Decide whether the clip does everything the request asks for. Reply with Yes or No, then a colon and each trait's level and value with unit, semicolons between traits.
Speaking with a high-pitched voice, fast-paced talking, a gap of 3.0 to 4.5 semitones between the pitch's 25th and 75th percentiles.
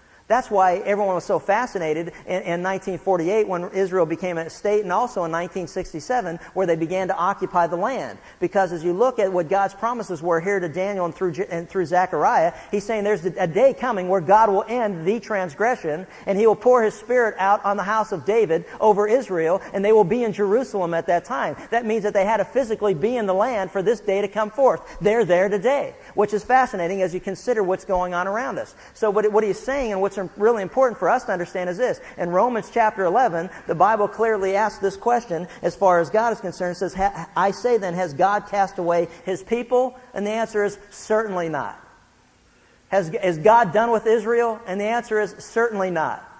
Yes: high, 200 Hz; fast, 215 wpm; average, 3.3 semitones